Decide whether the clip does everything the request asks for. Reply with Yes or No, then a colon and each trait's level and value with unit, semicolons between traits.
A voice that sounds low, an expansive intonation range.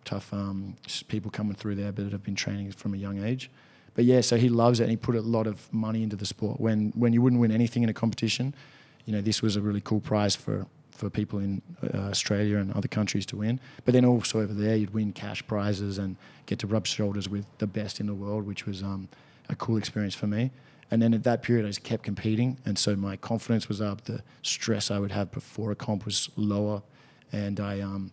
No: low, 105 Hz; narrow, 2.6 semitones